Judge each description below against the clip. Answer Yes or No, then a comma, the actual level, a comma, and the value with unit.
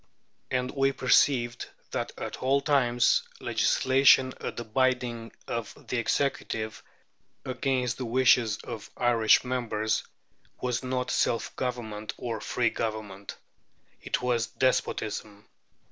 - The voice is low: Yes, low, 120 Hz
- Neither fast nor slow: No, slow, 115 wpm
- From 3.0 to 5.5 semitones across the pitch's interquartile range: No, narrow, 2.5 semitones